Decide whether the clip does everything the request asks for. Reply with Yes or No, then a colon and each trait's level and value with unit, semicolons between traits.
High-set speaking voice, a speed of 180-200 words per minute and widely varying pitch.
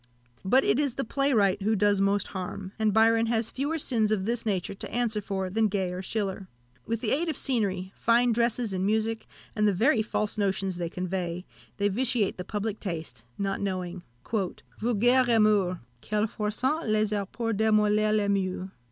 No: high, 210 Hz; average, 185 wpm; average, 2.9 semitones